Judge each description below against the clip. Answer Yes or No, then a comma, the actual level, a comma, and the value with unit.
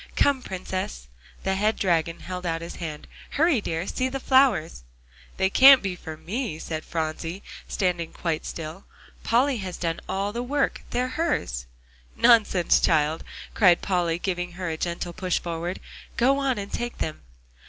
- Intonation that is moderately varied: No, wide, 6.1 semitones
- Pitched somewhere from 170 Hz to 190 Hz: Yes, medium, 185 Hz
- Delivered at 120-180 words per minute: Yes, average, 160 wpm